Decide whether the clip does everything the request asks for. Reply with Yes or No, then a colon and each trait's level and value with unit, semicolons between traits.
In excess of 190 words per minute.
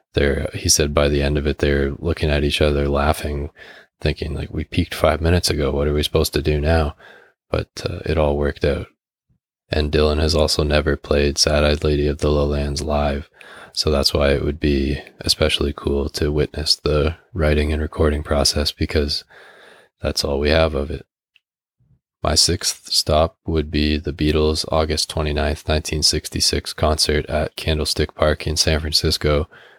No: average, 175 wpm